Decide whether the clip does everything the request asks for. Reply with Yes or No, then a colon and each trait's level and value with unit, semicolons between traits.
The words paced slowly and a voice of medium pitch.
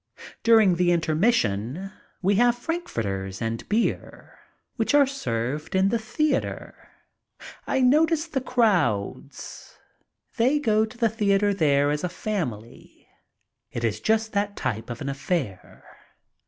No: slow, 130 wpm; high, 195 Hz